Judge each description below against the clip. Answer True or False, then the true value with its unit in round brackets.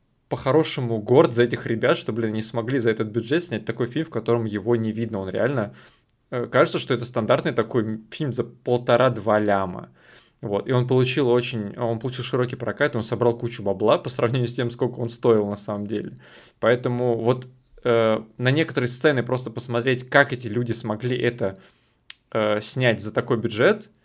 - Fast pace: True (180 wpm)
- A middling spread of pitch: False (2.2 semitones)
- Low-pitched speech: True (120 Hz)